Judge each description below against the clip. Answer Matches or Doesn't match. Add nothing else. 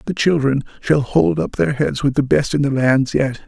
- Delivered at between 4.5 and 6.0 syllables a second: Matches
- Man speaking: Matches